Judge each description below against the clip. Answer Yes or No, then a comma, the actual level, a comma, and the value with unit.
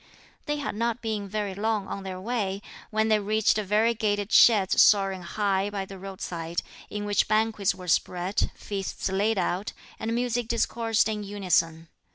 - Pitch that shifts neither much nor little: No, narrow, 2.3 semitones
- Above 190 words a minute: No, average, 160 wpm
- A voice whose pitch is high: Yes, high, 205 Hz